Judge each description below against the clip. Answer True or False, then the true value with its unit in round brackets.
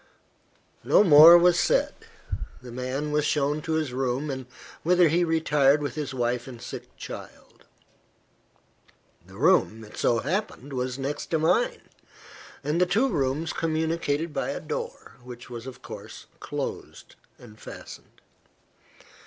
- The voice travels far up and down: False (4.5 semitones)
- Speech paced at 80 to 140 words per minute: True (135 wpm)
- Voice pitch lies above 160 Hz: False (145 Hz)